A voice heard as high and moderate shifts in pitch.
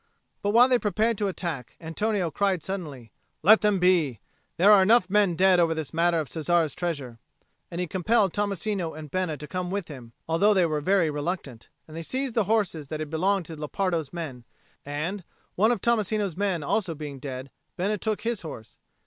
No: medium, 175 Hz; average, 4.6 semitones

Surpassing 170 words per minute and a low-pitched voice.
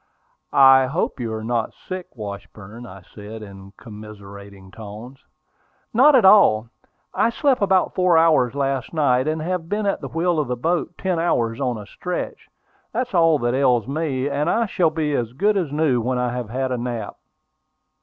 Yes: average, 185 wpm; low, 130 Hz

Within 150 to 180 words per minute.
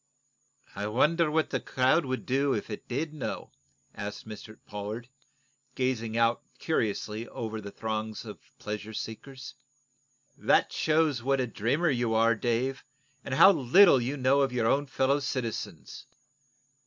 No: average, 140 wpm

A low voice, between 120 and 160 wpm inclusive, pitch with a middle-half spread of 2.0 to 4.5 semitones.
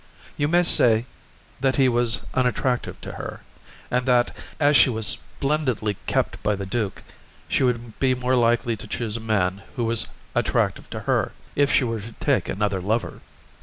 No: low, 120 Hz; average, 175 wpm; average, 2.9 semitones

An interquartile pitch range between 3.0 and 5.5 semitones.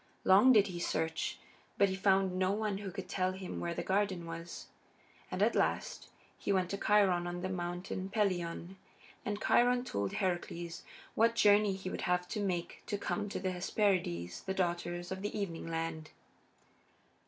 No: narrow, 2.6 semitones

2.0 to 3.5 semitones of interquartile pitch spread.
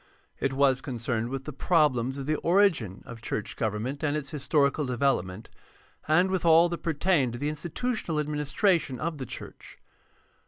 No: average, 4.2 semitones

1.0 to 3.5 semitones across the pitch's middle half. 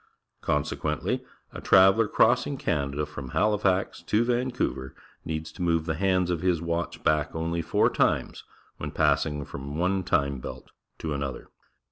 No: average, 4.7 semitones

